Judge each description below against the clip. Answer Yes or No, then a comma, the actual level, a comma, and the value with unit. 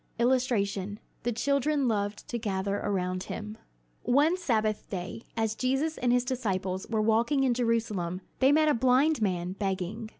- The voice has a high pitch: Yes, high, 225 Hz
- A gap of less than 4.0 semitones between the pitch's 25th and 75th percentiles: No, average, 4.3 semitones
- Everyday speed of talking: Yes, average, 155 wpm